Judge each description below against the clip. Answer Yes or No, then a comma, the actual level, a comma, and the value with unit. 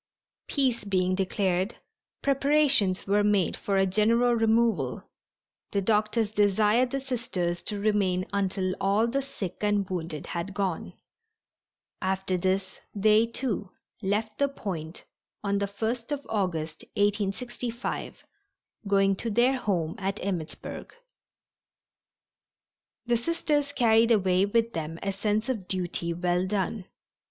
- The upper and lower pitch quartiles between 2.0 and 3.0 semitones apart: No, average, 3.6 semitones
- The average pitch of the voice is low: No, high, 205 Hz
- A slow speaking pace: Yes, slow, 125 wpm